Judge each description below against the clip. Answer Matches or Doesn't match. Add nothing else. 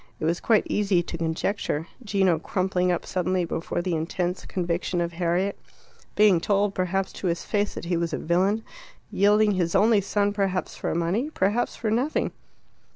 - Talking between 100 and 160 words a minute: Doesn't match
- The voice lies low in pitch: Doesn't match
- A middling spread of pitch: Matches